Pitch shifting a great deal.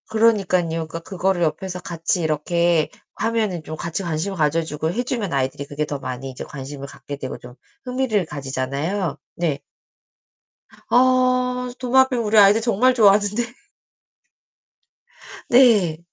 Yes: wide, 6.7 semitones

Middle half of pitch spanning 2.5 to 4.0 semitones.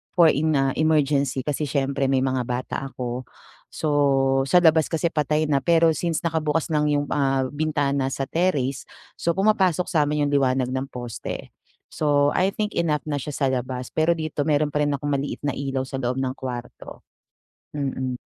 Yes: average, 2.9 semitones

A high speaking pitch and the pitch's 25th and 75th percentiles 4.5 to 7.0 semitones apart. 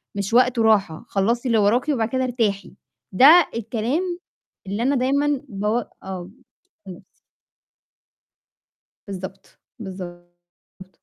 Yes: high, 220 Hz; average, 4.9 semitones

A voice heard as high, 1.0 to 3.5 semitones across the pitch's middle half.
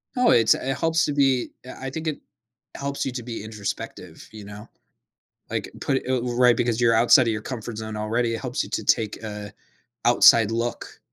No: low, 120 Hz; average, 3.2 semitones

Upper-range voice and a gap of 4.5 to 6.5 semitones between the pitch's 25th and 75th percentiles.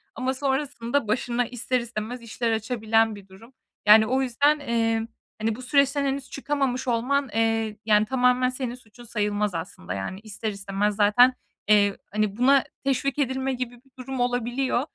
No: high, 240 Hz; average, 3.4 semitones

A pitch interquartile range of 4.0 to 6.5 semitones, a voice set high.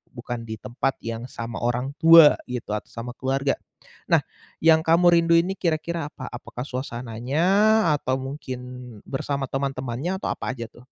No: average, 4.6 semitones; low, 130 Hz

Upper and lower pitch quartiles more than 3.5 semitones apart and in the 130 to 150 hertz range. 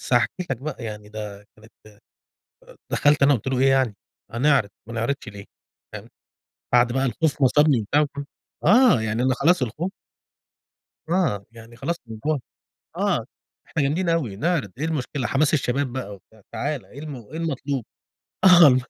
Yes: average, 5.0 semitones; low, 135 Hz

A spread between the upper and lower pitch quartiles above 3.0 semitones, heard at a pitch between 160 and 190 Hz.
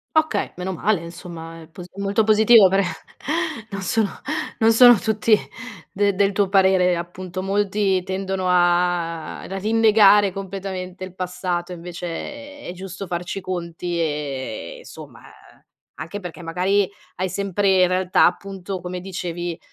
No: narrow, 2.1 semitones; medium, 185 Hz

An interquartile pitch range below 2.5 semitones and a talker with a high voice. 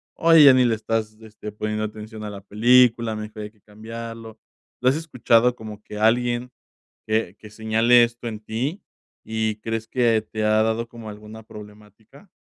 No: narrow, 1.8 semitones; low, 110 Hz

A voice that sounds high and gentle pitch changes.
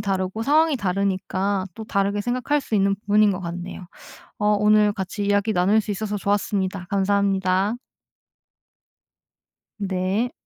Yes: high, 200 Hz; narrow, 1.8 semitones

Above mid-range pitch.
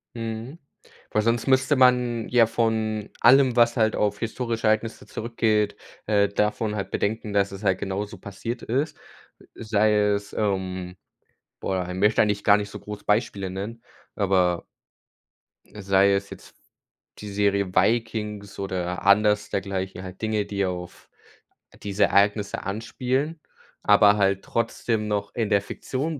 No: low, 105 Hz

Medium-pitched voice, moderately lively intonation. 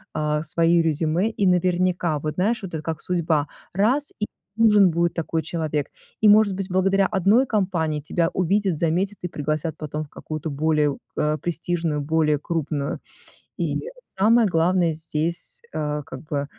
Yes: medium, 165 Hz; average, 3.6 semitones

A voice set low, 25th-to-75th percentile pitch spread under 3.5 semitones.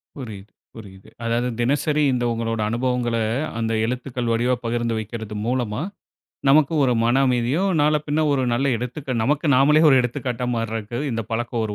Yes: low, 120 Hz; average, 2.9 semitones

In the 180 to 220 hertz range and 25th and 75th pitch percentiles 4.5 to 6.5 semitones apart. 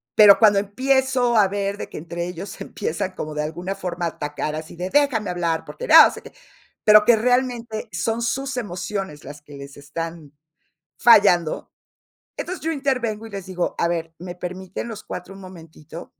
Yes: high, 190 Hz; average, 4.9 semitones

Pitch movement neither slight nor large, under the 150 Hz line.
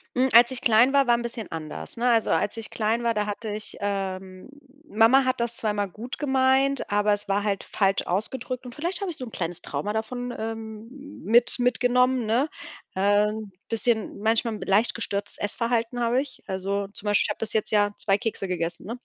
No: average, 3.3 semitones; high, 225 Hz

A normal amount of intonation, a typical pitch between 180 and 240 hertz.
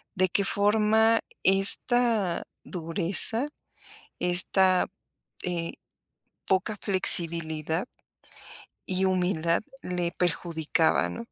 Yes: average, 3.1 semitones; medium, 185 Hz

